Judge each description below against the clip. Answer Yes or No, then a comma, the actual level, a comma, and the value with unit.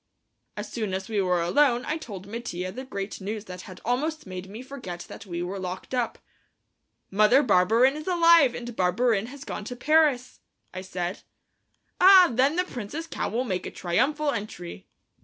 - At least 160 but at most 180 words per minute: Yes, average, 175 wpm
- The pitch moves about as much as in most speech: No, wide, 6.6 semitones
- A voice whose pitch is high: Yes, high, 225 Hz